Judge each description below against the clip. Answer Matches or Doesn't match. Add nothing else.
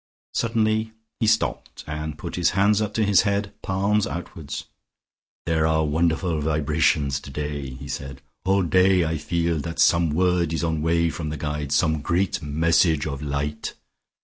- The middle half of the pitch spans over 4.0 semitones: Doesn't match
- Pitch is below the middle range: Matches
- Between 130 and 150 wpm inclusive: Doesn't match